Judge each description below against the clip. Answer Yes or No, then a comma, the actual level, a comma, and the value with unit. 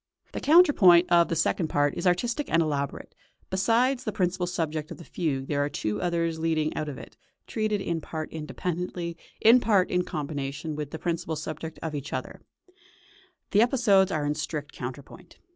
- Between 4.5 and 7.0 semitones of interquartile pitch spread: No, average, 3.7 semitones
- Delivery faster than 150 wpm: Yes, average, 175 wpm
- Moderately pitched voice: Yes, medium, 165 Hz